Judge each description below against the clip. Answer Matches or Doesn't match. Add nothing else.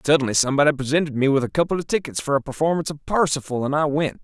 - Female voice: Doesn't match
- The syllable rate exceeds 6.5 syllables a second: Matches